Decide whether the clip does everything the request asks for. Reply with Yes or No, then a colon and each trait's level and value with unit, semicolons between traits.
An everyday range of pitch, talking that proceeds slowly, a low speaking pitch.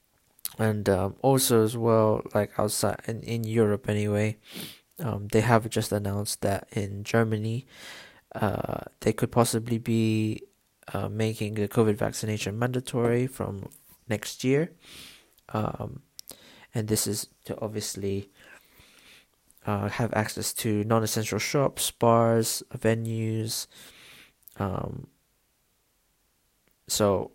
No: narrow, 1.8 semitones; slow, 110 wpm; low, 110 Hz